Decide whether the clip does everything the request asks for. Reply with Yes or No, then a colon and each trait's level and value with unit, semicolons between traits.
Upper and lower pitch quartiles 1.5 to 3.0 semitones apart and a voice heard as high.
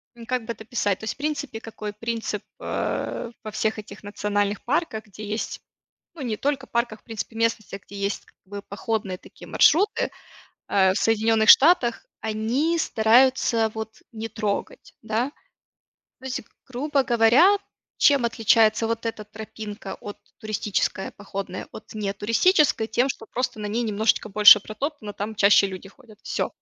Yes: narrow, 2.6 semitones; high, 220 Hz